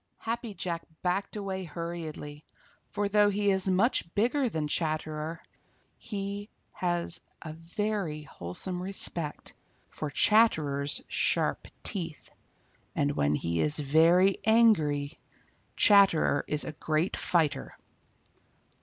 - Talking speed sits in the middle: No, slow, 110 wpm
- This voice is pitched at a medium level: Yes, medium, 170 Hz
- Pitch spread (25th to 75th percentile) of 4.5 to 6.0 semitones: Yes, average, 4.8 semitones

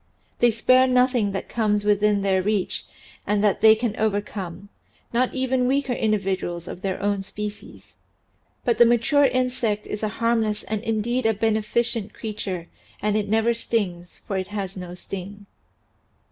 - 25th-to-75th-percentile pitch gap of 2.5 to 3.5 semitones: Yes, average, 2.9 semitones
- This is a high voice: Yes, high, 210 Hz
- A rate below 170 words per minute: Yes, average, 155 wpm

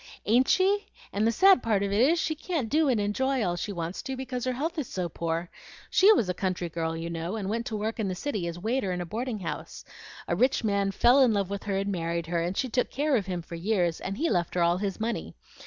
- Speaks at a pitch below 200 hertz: No, high, 205 Hz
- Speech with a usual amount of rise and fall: No, wide, 6.3 semitones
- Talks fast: Yes, fast, 270 wpm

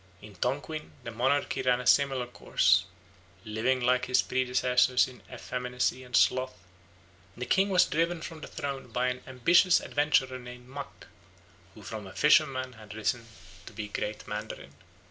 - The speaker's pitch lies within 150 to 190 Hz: No, low, 125 Hz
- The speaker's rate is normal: Yes, average, 155 wpm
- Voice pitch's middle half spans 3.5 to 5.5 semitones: No, narrow, 2.4 semitones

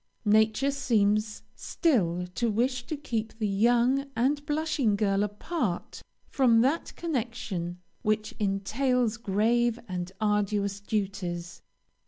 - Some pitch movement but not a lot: Yes, average, 3.8 semitones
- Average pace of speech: No, slow, 110 wpm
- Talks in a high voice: Yes, high, 220 Hz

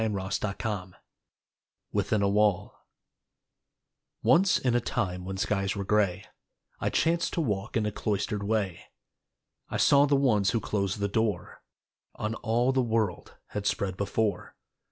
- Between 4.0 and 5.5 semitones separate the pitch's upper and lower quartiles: No, narrow, 2.6 semitones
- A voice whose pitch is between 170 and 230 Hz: No, low, 105 Hz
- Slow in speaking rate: No, average, 145 wpm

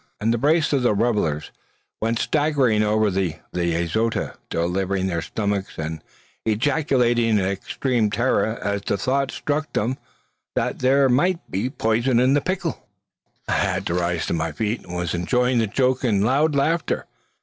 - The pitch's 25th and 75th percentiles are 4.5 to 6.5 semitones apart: Yes, average, 5.2 semitones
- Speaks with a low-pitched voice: Yes, low, 110 Hz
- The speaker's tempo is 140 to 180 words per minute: Yes, average, 155 wpm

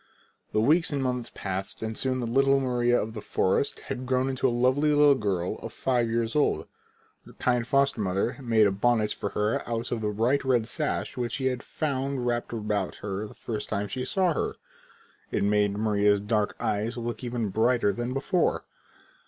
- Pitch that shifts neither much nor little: Yes, average, 3.7 semitones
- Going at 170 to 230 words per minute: Yes, average, 190 wpm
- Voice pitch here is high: No, low, 120 Hz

